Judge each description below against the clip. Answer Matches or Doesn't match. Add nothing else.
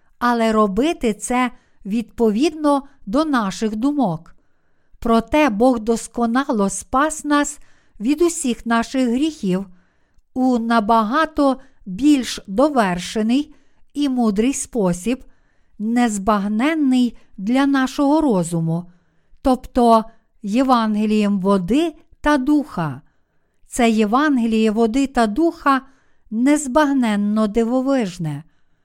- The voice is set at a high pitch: Matches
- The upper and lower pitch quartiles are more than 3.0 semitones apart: Matches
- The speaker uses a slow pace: Matches